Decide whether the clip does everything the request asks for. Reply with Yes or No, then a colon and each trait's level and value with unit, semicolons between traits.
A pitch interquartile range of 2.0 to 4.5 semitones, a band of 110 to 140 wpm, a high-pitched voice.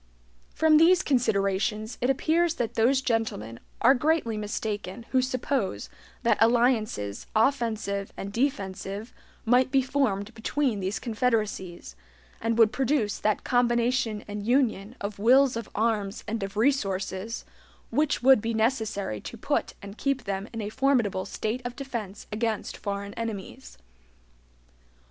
Yes: average, 4.0 semitones; slow, 135 wpm; high, 225 Hz